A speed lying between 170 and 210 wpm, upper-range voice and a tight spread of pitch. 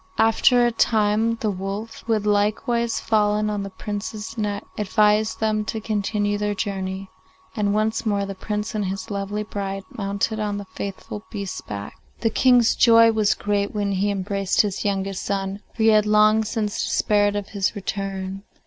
Yes: average, 175 wpm; high, 210 Hz; narrow, 1.6 semitones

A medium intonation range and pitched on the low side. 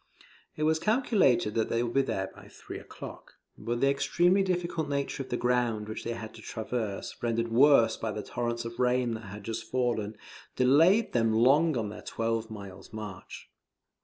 Yes: average, 3.8 semitones; low, 120 Hz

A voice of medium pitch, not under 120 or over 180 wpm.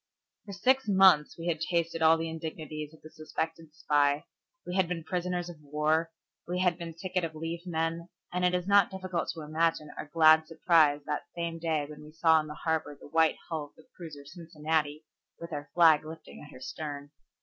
No: medium, 160 Hz; fast, 205 wpm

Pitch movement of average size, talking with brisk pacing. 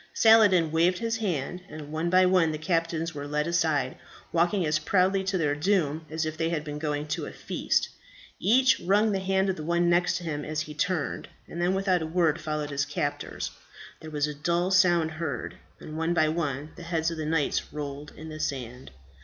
Yes: average, 3.1 semitones; fast, 210 wpm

